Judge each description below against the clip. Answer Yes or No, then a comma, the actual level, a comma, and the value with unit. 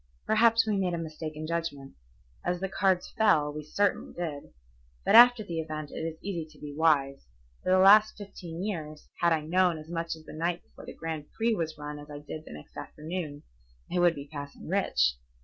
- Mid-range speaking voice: Yes, medium, 165 Hz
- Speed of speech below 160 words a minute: No, fast, 205 wpm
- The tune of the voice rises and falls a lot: No, average, 3.6 semitones